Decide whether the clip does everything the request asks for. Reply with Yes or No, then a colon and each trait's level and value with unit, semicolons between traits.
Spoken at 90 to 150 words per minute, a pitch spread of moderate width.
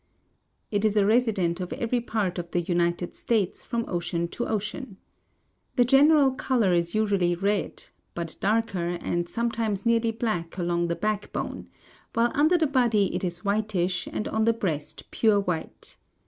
No: average, 160 wpm; average, 4.8 semitones